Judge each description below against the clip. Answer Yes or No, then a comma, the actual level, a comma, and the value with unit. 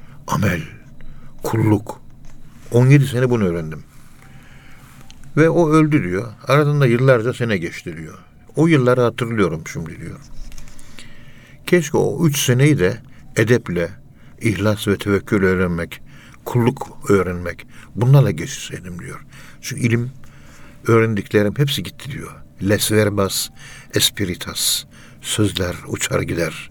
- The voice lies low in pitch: Yes, low, 120 Hz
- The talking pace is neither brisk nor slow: Yes, average, 105 wpm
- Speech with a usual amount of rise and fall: Yes, average, 4.7 semitones